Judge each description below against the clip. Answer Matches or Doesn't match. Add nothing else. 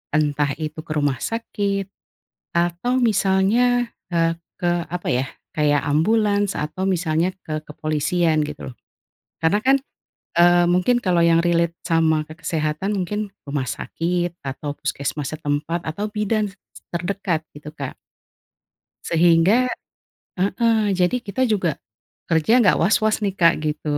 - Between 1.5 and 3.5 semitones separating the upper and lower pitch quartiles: Doesn't match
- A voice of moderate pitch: Matches